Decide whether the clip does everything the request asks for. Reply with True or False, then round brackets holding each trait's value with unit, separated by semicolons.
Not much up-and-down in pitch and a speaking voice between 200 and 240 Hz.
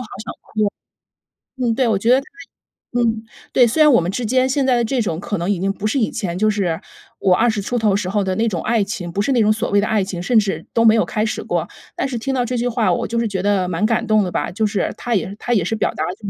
False (3.3 semitones; 215 Hz)